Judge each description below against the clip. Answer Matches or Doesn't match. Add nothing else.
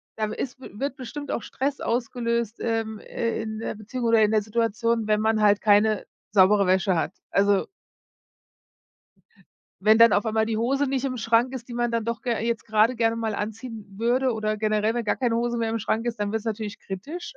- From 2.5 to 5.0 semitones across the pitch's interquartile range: Doesn't match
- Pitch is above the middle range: Matches